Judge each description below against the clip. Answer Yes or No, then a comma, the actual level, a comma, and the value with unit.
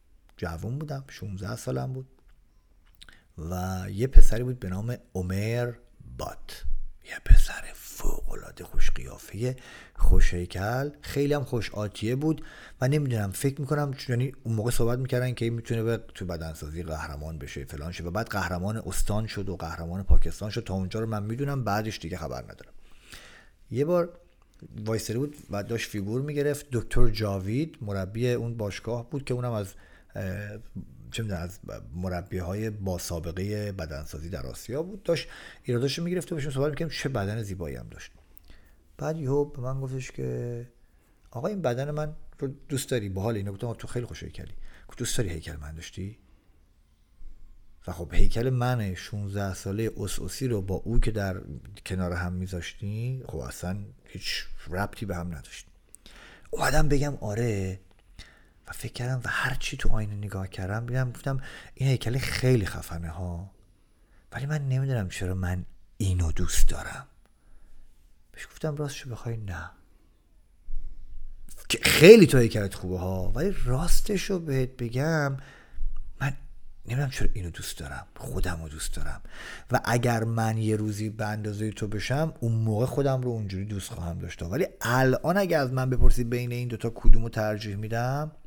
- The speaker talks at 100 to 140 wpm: No, fast, 155 wpm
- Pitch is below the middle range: Yes, low, 105 Hz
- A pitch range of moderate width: No, wide, 6.1 semitones